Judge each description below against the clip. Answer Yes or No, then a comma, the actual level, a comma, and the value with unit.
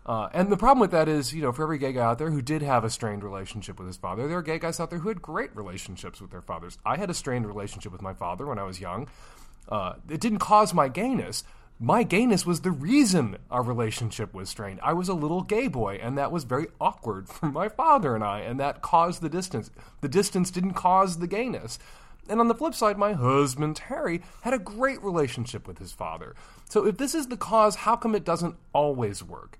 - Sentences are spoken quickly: Yes, fast, 240 wpm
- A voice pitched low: No, medium, 155 Hz